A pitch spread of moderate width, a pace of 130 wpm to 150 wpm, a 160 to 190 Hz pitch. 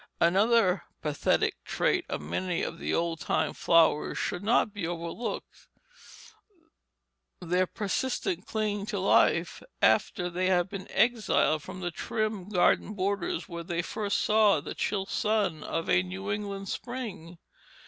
Yes: average, 3.8 semitones; average, 140 wpm; medium, 185 Hz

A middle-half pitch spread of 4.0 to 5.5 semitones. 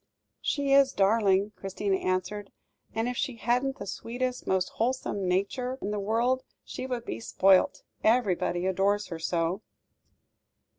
Yes: average, 4.6 semitones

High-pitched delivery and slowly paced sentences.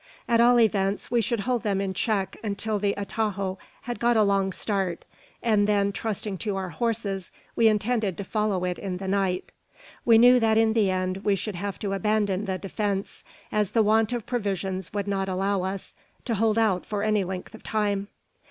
No: high, 205 Hz; average, 200 wpm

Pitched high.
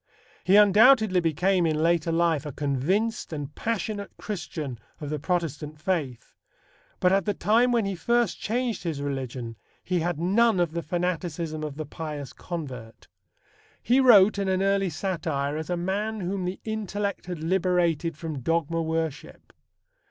No: medium, 175 Hz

